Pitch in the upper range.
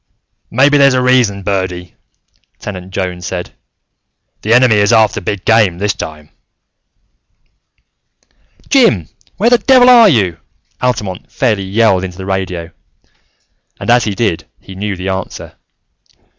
No: low, 100 Hz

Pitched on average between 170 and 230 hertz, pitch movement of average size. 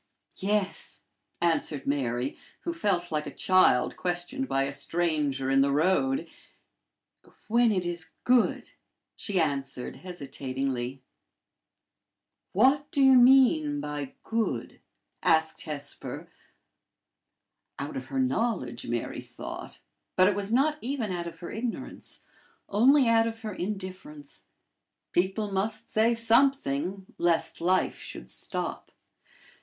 No: medium, 185 Hz; wide, 8.0 semitones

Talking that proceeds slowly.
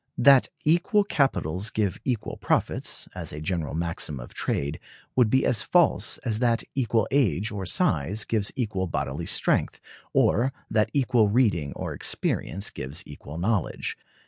No: average, 145 wpm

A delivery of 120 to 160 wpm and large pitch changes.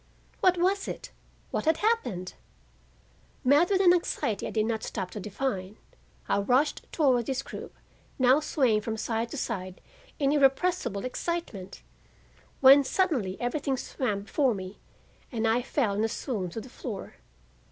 Yes: average, 150 wpm; wide, 5.7 semitones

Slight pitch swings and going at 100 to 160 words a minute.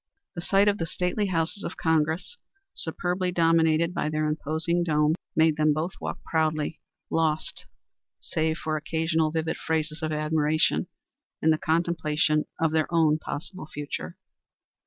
Yes: narrow, 1.5 semitones; average, 140 wpm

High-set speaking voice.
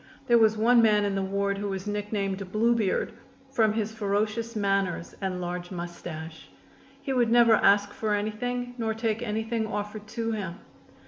Yes: high, 210 Hz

